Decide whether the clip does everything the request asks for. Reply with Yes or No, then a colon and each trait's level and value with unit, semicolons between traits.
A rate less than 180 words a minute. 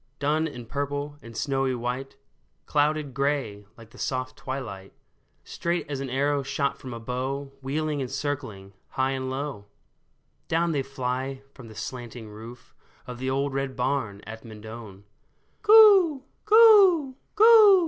Yes: average, 150 wpm